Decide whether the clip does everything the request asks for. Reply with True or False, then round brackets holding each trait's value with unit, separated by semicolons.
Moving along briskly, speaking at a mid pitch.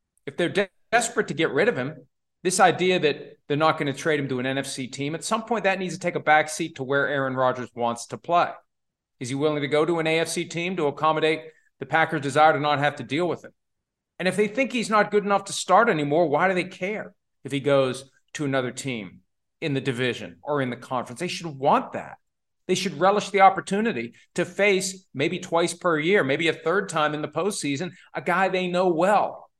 True (235 wpm; 160 Hz)